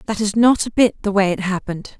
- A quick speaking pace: Yes, fast, 270 wpm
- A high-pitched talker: Yes, high, 205 Hz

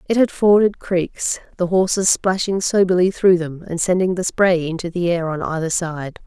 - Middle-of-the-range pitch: Yes, medium, 180 Hz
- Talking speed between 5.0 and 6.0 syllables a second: No, 4.7 syllables/s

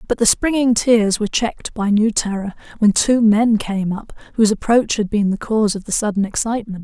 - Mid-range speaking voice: No, high, 215 Hz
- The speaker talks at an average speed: No, fast, 210 wpm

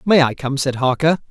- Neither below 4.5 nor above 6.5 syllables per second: Yes, 5.4 syllables/s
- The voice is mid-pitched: Yes, medium, 145 Hz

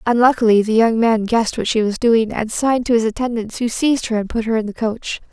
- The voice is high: Yes, high, 230 Hz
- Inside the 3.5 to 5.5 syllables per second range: No, 6.1 syllables/s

